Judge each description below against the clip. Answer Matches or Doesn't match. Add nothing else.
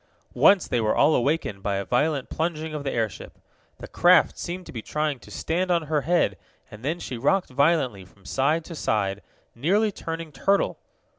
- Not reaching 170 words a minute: Doesn't match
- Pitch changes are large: Matches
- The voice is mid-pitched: Matches